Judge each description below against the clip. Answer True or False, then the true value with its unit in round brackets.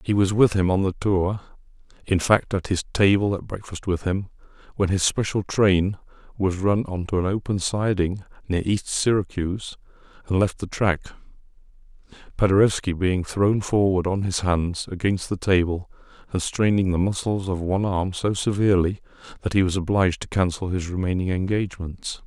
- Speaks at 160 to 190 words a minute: True (165 wpm)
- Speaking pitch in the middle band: False (95 Hz)